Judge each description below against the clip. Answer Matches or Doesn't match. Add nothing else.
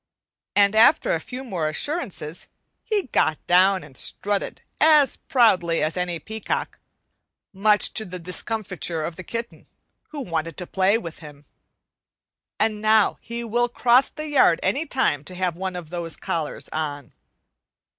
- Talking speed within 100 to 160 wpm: Matches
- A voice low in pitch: Doesn't match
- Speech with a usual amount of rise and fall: Doesn't match